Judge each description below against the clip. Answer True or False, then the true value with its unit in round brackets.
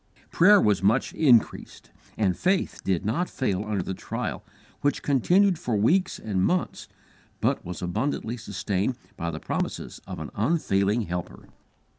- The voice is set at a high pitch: False (110 Hz)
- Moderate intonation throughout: False (7.4 semitones)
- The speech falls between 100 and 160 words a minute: True (145 wpm)